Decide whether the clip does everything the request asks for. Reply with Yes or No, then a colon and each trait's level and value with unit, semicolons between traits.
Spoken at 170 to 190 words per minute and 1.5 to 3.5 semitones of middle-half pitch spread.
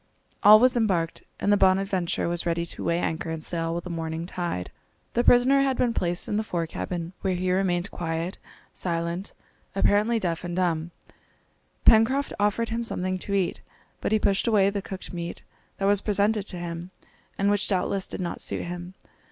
Yes: average, 185 wpm; average, 3.1 semitones